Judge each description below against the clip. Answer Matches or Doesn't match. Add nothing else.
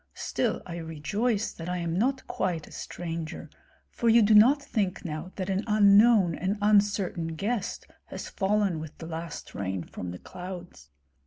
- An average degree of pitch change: Matches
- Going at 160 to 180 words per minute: Matches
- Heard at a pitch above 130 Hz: Matches